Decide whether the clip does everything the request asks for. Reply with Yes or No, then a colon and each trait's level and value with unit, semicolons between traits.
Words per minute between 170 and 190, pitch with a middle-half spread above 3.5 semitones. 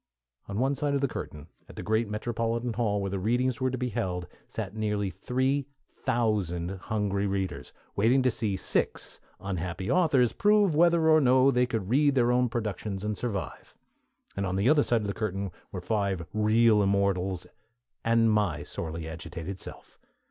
Yes: average, 175 wpm; average, 4.3 semitones